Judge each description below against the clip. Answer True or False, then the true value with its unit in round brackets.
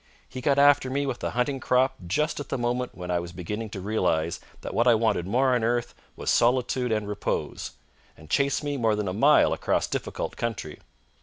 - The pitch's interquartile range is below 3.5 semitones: False (4.2 semitones)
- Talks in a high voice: False (120 Hz)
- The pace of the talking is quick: True (210 wpm)